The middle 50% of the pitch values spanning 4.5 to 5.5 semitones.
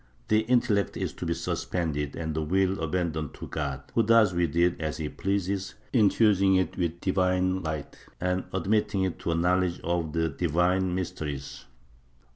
No: average, 3.0 semitones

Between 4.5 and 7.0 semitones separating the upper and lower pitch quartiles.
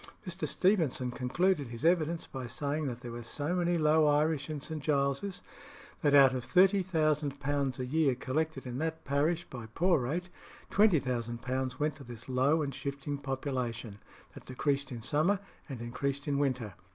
No: average, 3.8 semitones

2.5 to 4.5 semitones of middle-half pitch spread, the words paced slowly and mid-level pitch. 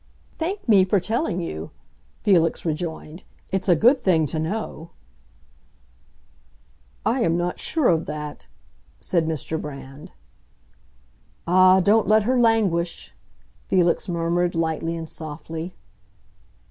Yes: average, 4.1 semitones; slow, 115 wpm; medium, 175 Hz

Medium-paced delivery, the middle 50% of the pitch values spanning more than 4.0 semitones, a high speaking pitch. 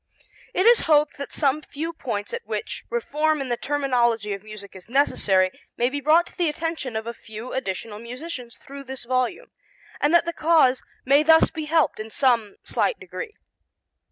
Yes: average, 185 wpm; average, 5.1 semitones; very high, 275 Hz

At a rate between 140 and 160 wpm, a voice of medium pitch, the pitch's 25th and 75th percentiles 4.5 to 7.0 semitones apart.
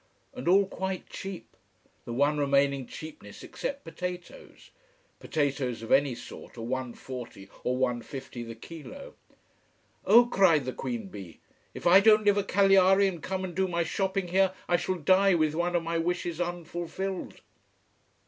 Yes: average, 155 wpm; medium, 175 Hz; wide, 5.5 semitones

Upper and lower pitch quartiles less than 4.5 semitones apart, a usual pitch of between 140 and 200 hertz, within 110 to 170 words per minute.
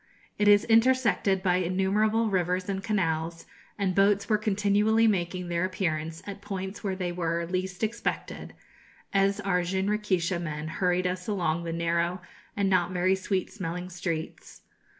Yes: average, 2.7 semitones; medium, 185 Hz; average, 150 wpm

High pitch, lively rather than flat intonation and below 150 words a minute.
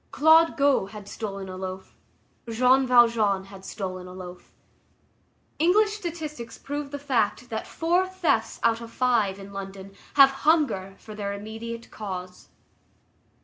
Yes: high, 225 Hz; wide, 6.5 semitones; average, 140 wpm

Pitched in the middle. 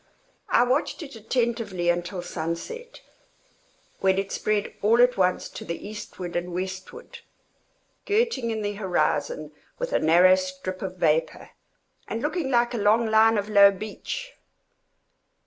No: high, 205 Hz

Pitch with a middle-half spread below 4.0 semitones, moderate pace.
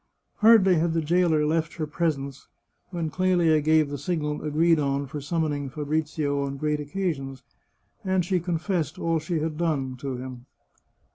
Yes: average, 3.0 semitones; average, 160 wpm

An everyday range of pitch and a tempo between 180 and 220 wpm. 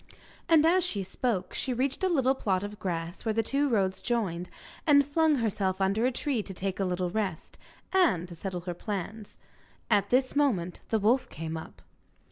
No: wide, 6.1 semitones; average, 190 wpm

